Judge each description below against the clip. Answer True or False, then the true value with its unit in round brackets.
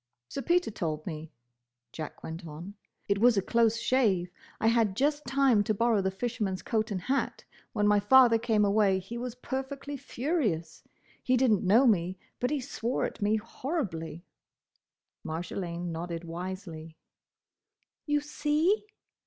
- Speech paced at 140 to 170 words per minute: True (150 wpm)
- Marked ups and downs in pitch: True (6.2 semitones)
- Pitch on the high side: True (215 Hz)